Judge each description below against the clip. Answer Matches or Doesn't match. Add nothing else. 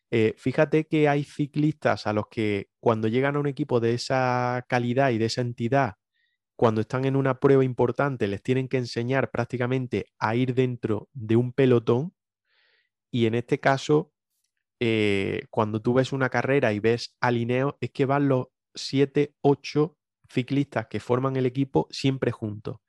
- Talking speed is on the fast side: Doesn't match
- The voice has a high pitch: Doesn't match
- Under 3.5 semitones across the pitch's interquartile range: Matches